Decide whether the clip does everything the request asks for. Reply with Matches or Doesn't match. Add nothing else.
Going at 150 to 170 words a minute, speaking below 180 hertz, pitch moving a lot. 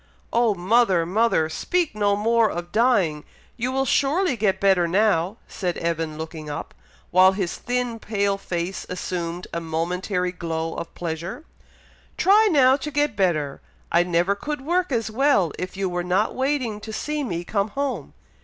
Doesn't match